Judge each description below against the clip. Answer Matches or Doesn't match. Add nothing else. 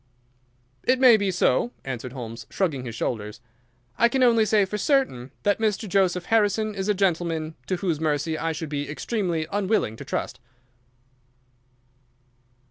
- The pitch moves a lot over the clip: Matches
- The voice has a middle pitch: Matches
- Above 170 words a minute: Doesn't match